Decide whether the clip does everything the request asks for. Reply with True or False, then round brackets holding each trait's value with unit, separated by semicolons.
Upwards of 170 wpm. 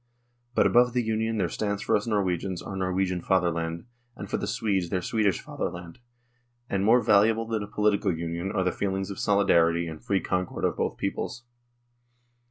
True (180 wpm)